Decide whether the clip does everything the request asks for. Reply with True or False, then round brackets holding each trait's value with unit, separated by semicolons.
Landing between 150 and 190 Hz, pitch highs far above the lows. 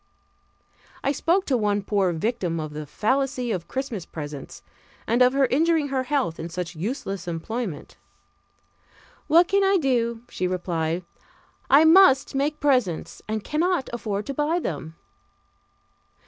False (235 Hz; 7.8 semitones)